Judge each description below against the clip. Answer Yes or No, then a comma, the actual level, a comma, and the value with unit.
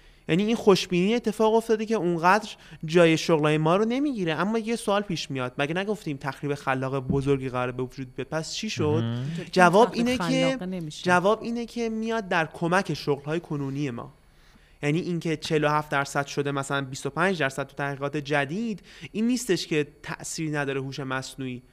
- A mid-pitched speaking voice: Yes, medium, 160 Hz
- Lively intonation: Yes, wide, 5.9 semitones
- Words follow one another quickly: Yes, fast, 165 wpm